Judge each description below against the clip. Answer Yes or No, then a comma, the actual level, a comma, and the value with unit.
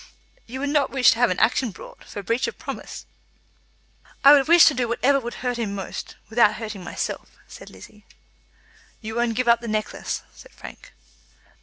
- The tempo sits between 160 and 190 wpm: Yes, average, 185 wpm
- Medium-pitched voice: No, high, 235 Hz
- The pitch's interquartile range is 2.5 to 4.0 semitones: Yes, average, 3.2 semitones